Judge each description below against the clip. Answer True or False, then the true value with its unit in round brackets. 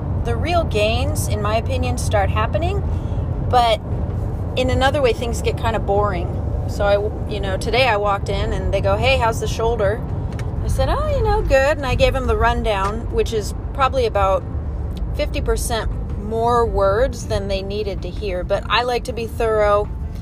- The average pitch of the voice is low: True (100 Hz)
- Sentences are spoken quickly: False (185 wpm)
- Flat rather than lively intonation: False (3.6 semitones)